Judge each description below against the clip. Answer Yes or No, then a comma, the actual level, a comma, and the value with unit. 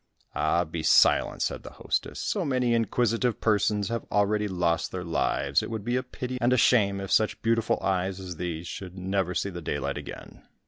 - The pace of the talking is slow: No, average, 195 wpm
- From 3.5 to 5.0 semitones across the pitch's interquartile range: Yes, average, 4.2 semitones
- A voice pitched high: No, low, 100 Hz